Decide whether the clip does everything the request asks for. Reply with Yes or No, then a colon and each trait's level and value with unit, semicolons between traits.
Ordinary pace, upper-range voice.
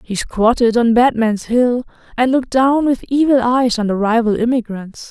Yes: average, 175 wpm; high, 240 Hz